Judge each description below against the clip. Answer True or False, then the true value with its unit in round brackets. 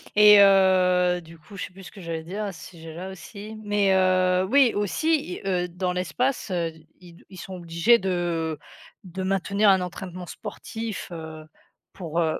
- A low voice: False (185 Hz)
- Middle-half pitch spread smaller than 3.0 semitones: True (2.5 semitones)